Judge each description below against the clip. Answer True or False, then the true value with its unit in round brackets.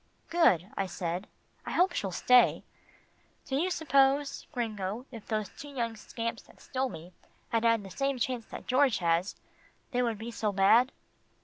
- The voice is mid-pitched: False (230 Hz)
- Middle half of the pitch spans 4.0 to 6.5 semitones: True (4.8 semitones)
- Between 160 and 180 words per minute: True (170 wpm)